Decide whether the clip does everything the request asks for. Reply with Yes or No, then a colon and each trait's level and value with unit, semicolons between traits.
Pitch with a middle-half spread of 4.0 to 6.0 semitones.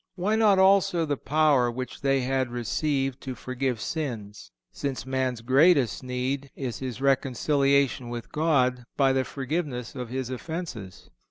No: average, 2.7 semitones